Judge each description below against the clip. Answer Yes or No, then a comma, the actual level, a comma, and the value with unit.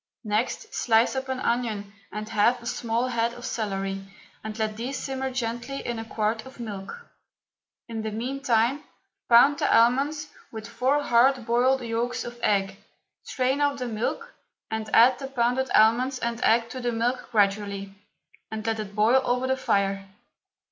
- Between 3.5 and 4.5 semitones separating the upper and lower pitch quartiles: No, average, 3.0 semitones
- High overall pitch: Yes, high, 235 Hz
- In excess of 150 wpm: Yes, average, 165 wpm